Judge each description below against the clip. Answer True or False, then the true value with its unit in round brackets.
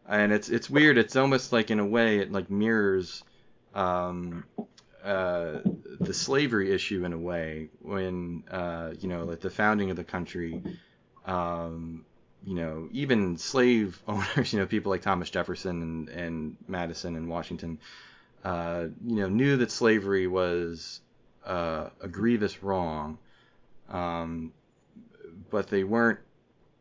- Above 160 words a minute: False (140 wpm)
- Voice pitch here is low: True (95 Hz)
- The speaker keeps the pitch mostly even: False (3.7 semitones)